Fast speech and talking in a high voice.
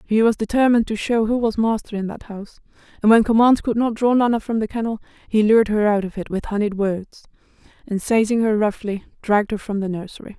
Yes: fast, 225 wpm; high, 215 Hz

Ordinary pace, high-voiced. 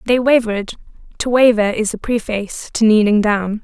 Yes: average, 150 wpm; high, 220 Hz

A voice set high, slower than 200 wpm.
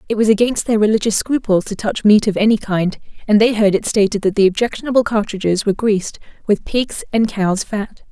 No: high, 210 Hz; fast, 205 wpm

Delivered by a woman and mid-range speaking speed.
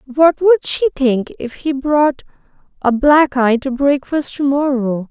Yes: female; average, 165 wpm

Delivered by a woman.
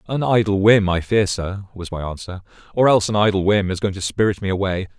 No: male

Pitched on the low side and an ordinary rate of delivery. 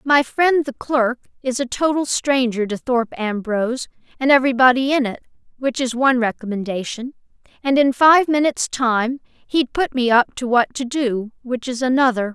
No: very high, 250 Hz; average, 170 wpm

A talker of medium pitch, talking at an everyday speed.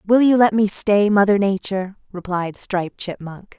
No: high, 200 Hz; average, 165 wpm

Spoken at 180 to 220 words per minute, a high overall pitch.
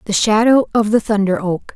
Yes: fast, 205 wpm; high, 210 Hz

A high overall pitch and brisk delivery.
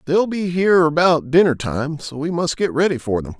No: medium, 155 Hz; fast, 230 wpm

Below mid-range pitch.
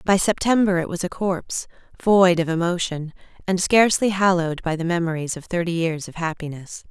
No: medium, 175 Hz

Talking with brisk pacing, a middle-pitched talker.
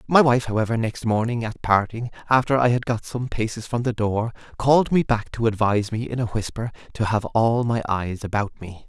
No: fast, 215 wpm; low, 115 Hz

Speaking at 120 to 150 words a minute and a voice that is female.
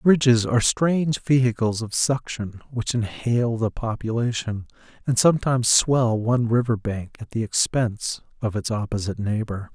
No: average, 140 wpm; male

